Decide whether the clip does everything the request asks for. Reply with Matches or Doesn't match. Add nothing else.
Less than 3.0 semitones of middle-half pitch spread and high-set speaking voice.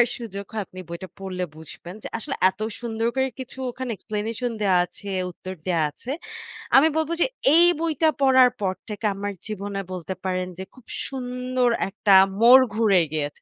Doesn't match